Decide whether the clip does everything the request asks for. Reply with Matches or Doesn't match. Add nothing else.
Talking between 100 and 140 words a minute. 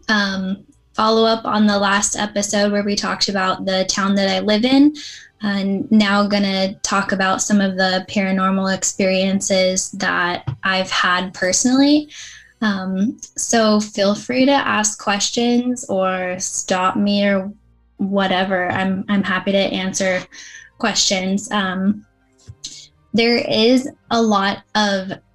Matches